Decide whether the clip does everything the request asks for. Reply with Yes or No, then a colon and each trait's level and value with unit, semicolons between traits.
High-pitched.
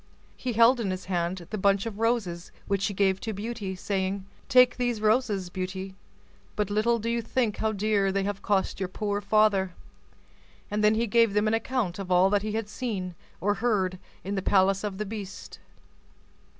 Yes: high, 205 Hz